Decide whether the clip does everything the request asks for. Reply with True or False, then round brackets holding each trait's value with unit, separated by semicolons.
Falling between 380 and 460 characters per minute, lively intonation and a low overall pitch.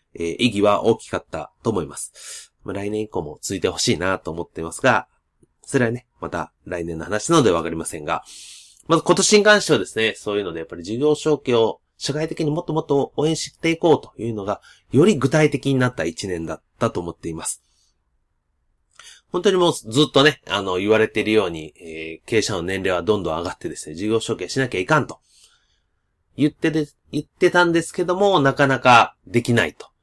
True (400 characters per minute; 8.8 semitones; 115 Hz)